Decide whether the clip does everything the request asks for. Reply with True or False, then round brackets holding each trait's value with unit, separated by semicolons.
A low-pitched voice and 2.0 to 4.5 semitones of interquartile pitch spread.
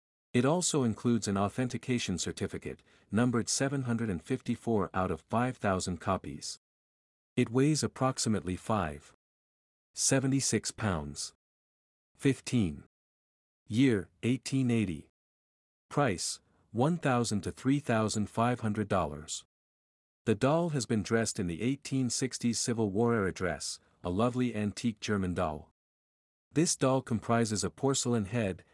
False (110 Hz; 5.3 semitones)